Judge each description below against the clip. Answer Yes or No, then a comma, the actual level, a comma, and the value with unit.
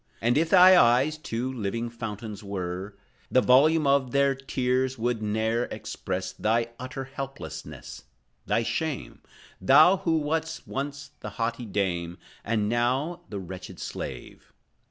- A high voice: No, low, 120 Hz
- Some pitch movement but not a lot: Yes, average, 4.5 semitones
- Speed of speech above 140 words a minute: No, slow, 135 wpm